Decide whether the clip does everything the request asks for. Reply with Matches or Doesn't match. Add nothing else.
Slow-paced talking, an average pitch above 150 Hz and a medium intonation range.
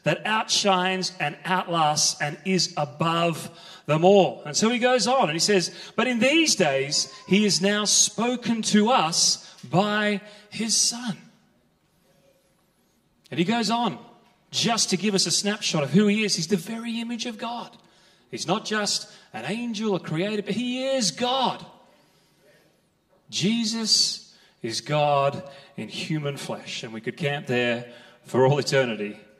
Doesn't match